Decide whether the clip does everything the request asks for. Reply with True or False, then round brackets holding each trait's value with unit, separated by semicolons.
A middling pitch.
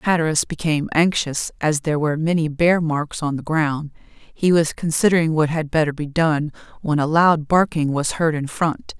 True (155 Hz)